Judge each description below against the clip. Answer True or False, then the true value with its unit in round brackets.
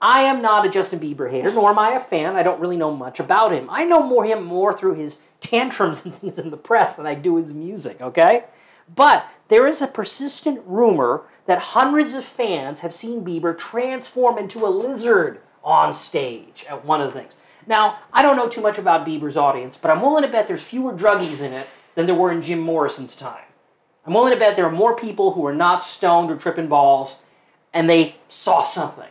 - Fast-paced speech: True (220 wpm)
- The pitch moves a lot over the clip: True (6.6 semitones)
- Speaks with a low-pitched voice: False (190 Hz)